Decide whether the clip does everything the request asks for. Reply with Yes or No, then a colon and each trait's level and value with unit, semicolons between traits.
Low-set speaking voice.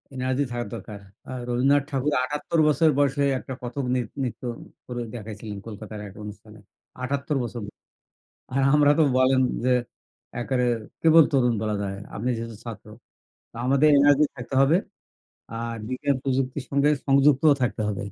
Yes: low, 130 Hz